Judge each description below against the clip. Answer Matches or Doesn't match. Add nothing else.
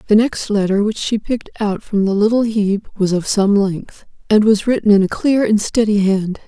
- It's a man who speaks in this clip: Doesn't match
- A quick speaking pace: Matches